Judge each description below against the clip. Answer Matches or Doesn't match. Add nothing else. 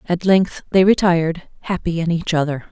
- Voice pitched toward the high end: Doesn't match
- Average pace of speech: Matches